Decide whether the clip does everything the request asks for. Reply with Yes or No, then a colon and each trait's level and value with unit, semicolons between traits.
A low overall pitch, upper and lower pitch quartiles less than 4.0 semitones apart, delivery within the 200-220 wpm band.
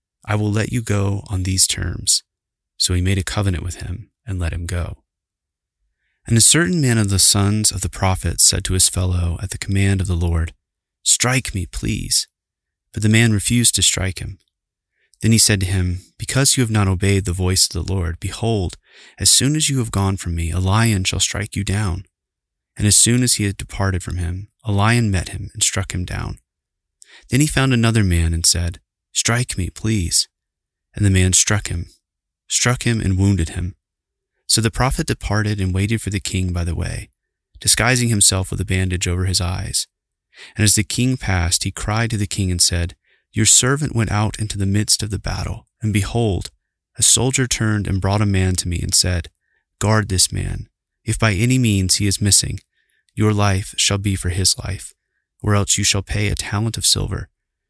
Yes: low, 100 Hz; average, 3.1 semitones; fast, 205 wpm